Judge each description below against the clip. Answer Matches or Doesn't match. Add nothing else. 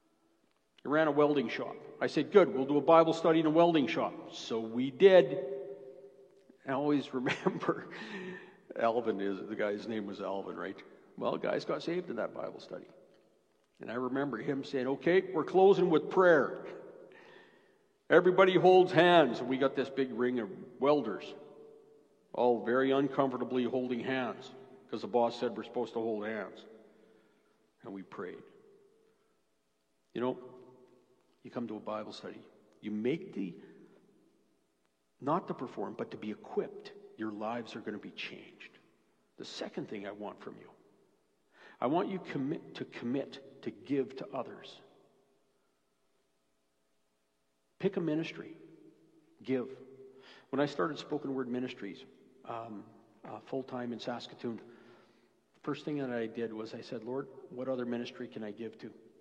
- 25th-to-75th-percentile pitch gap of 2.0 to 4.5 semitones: Doesn't match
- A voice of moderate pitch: Doesn't match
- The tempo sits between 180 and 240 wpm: Doesn't match